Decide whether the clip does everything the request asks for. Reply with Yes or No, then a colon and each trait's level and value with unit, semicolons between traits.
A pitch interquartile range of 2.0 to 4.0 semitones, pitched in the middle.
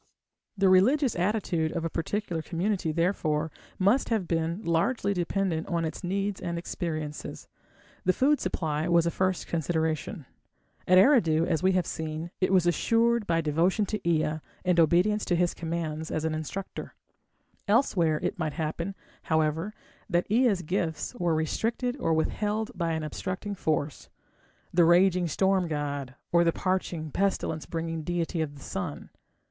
Yes: average, 3.4 semitones; medium, 170 Hz